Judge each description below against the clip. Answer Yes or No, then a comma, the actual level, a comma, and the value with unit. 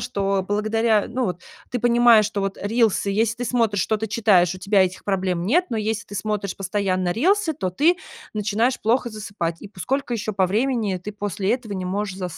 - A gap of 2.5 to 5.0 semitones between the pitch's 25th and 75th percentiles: Yes, average, 3.2 semitones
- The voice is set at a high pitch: Yes, high, 210 Hz